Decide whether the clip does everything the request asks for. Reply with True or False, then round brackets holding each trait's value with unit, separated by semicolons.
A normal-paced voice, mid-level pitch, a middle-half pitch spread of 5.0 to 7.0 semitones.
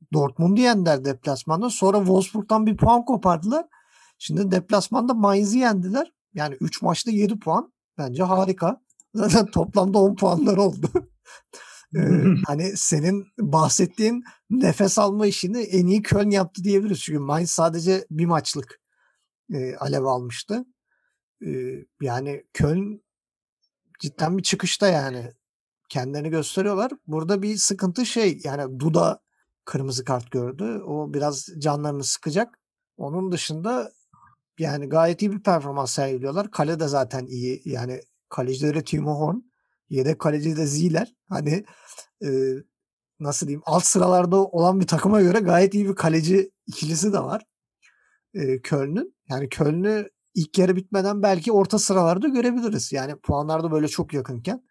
True (130 wpm; 180 Hz; 5.5 semitones)